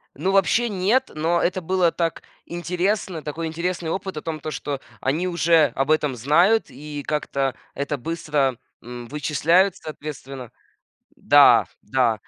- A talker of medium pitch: Yes, medium, 155 Hz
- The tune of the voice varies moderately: Yes, average, 4.1 semitones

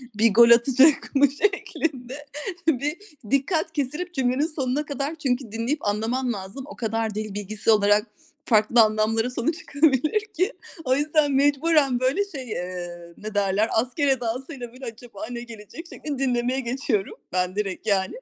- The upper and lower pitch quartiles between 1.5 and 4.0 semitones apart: No, average, 4.9 semitones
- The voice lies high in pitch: Yes, very high, 250 Hz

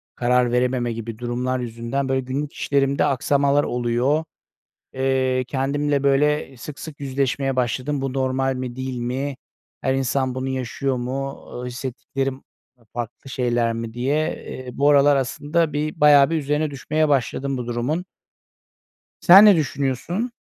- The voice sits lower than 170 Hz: Yes, low, 135 Hz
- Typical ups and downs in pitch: No, narrow, 2.3 semitones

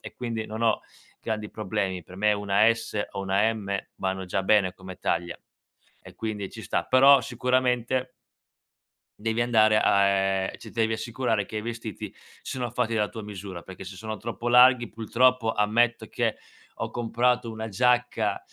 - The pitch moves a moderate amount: Yes, average, 3.1 semitones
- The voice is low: Yes, low, 110 Hz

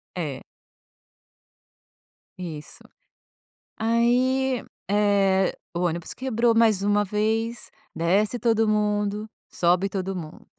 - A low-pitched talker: No, high, 210 Hz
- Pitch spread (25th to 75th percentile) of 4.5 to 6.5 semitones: No, average, 3.5 semitones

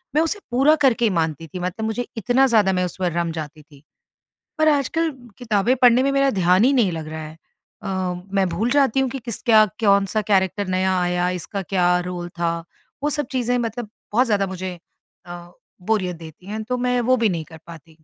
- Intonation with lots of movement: Yes, wide, 5.8 semitones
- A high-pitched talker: Yes, high, 200 Hz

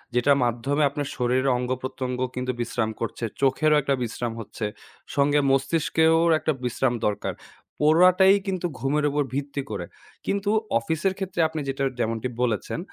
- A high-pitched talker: No, low, 135 Hz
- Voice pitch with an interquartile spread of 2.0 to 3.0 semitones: No, average, 4.1 semitones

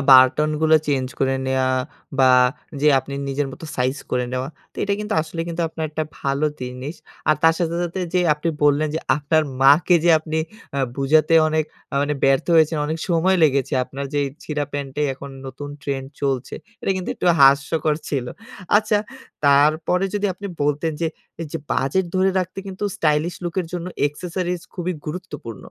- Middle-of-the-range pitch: Yes, medium, 150 Hz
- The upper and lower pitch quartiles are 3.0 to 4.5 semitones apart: Yes, average, 3.4 semitones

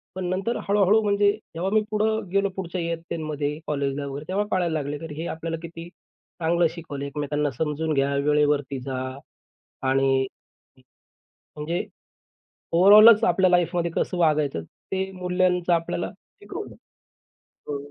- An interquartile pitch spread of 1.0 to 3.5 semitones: No, average, 4.2 semitones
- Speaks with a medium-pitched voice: Yes, medium, 165 Hz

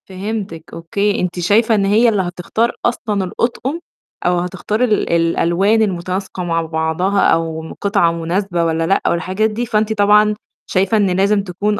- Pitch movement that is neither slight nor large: Yes, average, 3.6 semitones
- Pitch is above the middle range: Yes, high, 195 Hz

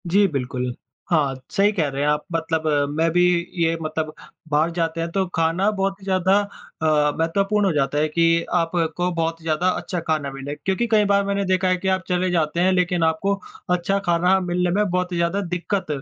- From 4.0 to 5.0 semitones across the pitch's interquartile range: No, average, 2.9 semitones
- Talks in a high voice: No, medium, 170 Hz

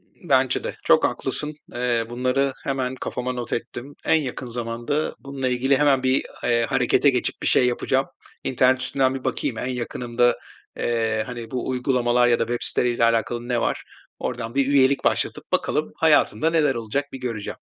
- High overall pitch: No, low, 125 Hz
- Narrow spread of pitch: Yes, narrow, 2.0 semitones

